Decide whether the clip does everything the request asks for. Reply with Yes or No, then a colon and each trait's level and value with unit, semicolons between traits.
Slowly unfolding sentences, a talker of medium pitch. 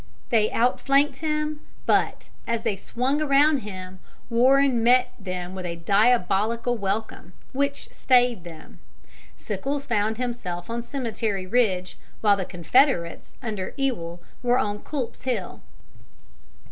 No: slow, 120 wpm; high, 230 Hz